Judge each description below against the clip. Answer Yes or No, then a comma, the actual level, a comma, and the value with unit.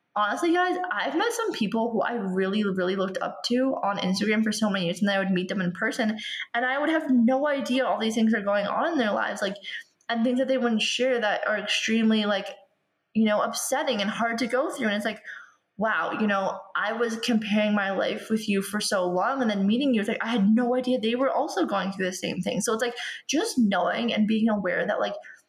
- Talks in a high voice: Yes, high, 220 Hz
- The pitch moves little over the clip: No, average, 3.5 semitones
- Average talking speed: No, fast, 245 wpm